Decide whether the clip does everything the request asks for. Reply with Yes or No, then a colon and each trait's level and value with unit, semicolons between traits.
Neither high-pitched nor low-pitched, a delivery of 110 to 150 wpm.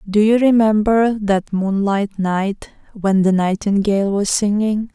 No: high, 205 Hz; slow, 135 wpm